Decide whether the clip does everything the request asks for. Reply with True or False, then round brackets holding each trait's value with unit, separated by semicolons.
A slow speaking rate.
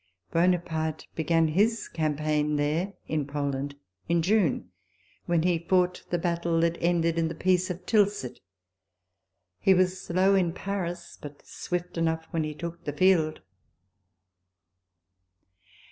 True (130 wpm)